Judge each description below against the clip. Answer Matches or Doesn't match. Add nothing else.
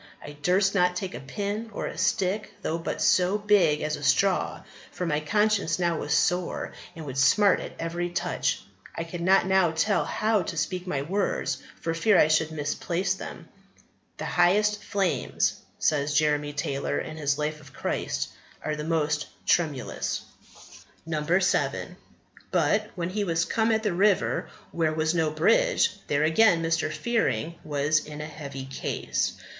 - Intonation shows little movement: Doesn't match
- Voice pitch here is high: Doesn't match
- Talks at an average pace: Matches